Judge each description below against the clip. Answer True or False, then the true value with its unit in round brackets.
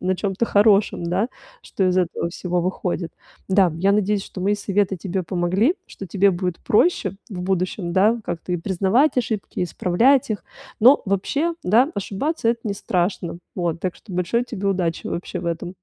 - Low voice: False (190 Hz)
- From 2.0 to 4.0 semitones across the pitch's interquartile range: True (2.9 semitones)